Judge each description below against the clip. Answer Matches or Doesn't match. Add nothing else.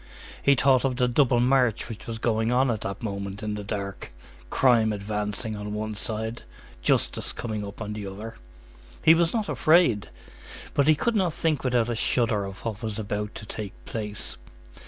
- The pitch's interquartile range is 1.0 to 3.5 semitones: Matches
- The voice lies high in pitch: Doesn't match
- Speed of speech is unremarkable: Matches